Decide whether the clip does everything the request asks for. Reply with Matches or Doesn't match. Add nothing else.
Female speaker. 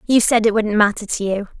Matches